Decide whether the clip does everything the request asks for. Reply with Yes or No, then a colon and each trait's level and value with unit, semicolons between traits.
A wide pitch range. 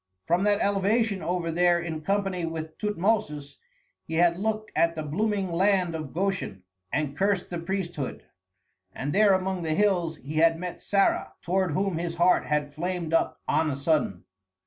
No: average, 3.5 semitones